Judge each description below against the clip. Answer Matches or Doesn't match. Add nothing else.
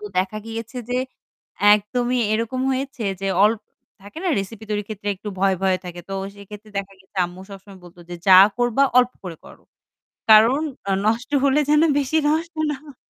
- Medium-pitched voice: Doesn't match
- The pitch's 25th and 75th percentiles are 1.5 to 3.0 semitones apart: Doesn't match